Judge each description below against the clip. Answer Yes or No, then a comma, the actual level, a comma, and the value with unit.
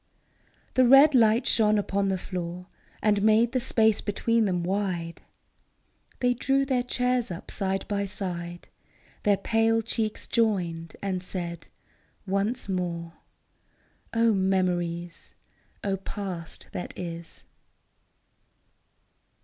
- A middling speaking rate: No, slow, 115 wpm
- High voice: Yes, high, 200 Hz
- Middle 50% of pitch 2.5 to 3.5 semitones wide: No, average, 4.1 semitones